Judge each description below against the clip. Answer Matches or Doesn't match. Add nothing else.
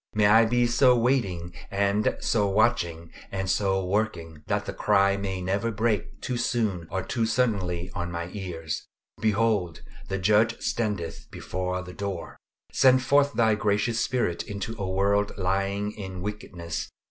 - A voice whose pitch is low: Matches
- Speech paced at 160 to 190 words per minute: Doesn't match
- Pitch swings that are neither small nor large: Matches